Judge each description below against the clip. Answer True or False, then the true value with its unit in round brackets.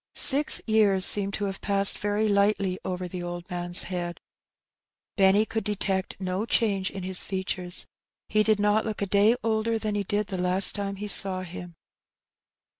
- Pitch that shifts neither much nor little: False (2.2 semitones)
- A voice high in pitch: True (200 Hz)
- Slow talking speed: False (175 wpm)